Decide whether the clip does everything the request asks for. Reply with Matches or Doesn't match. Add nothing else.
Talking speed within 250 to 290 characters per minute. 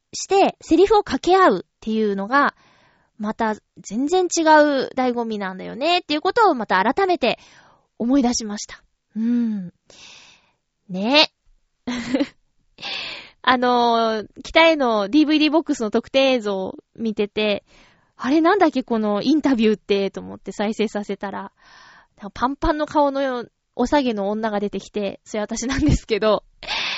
Matches